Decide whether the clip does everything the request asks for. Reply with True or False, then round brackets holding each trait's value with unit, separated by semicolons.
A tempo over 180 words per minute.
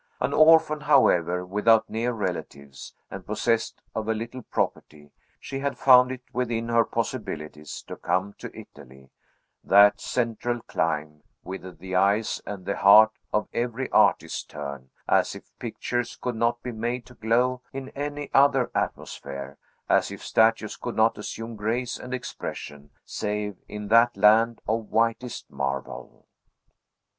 False (145 wpm)